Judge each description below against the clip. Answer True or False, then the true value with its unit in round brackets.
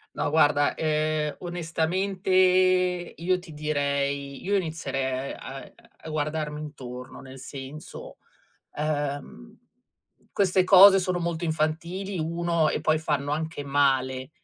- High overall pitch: False (155 Hz)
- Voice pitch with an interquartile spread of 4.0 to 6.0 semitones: False (3.2 semitones)